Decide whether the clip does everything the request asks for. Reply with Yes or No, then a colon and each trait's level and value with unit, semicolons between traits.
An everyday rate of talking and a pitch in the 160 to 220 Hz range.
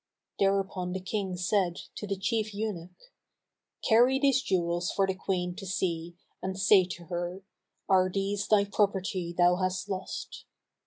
Yes: average, 150 wpm; high, 190 Hz